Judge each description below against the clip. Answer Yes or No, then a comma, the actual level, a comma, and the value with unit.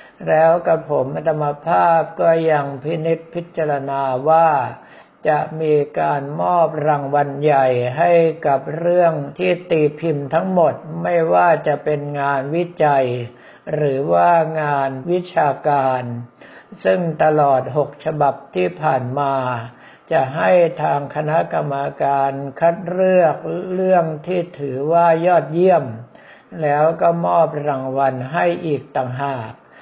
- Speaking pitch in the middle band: Yes, medium, 150 Hz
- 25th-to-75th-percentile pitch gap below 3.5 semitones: Yes, average, 3.1 semitones